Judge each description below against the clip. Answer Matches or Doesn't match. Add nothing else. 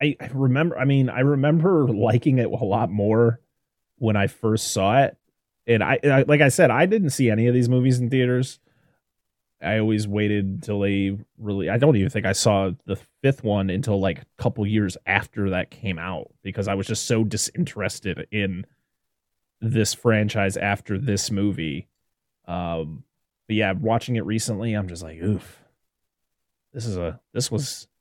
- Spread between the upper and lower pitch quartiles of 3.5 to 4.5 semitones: Matches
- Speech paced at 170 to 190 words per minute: Matches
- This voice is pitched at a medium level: Doesn't match